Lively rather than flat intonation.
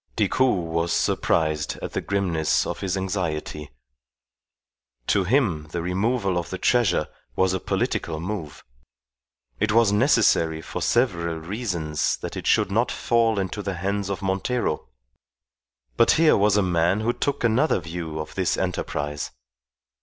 No: average, 4.5 semitones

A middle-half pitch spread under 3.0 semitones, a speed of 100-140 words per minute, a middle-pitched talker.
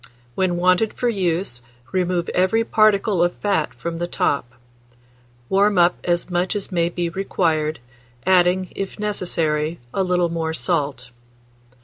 Yes: narrow, 2.4 semitones; slow, 135 wpm; medium, 175 Hz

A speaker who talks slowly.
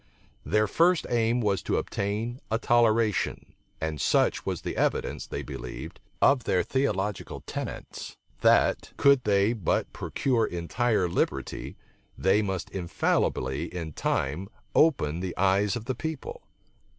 Yes: slow, 130 wpm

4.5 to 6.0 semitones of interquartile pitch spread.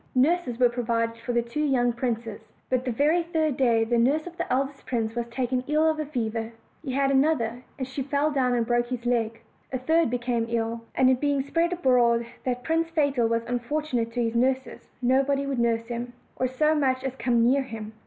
No: average, 3.0 semitones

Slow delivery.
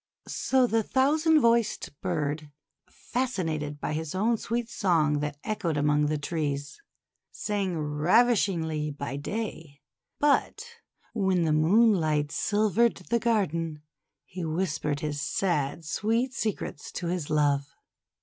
Yes: slow, 120 wpm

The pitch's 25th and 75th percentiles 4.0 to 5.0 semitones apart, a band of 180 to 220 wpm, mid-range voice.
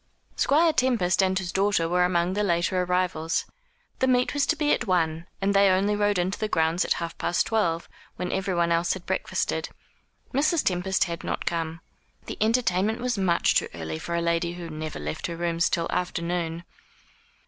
No: average, 3.3 semitones; average, 190 wpm; medium, 180 Hz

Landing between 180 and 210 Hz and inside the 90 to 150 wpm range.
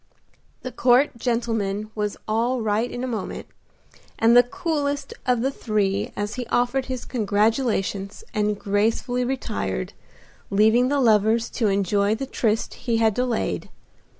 No: high, 230 Hz; average, 140 wpm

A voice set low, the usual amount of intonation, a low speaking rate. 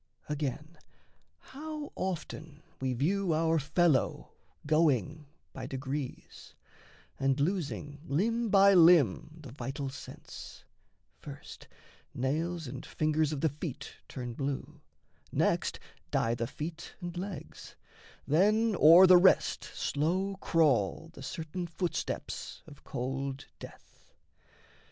No: medium, 155 Hz; average, 4.3 semitones; slow, 110 wpm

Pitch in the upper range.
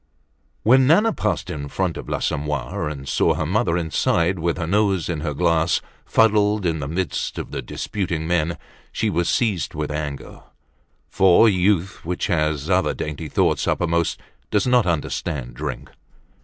No: very low, 85 Hz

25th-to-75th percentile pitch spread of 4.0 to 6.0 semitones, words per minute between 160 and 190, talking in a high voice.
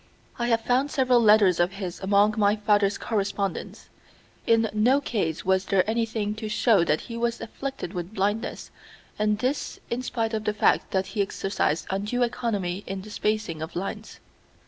No: average, 2.9 semitones; average, 170 wpm; high, 210 Hz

